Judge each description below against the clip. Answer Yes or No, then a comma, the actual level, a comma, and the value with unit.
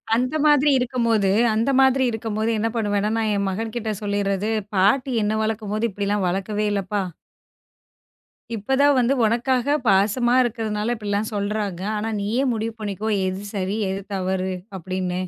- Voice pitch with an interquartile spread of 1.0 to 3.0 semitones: Yes, average, 2.7 semitones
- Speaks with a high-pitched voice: Yes, high, 215 Hz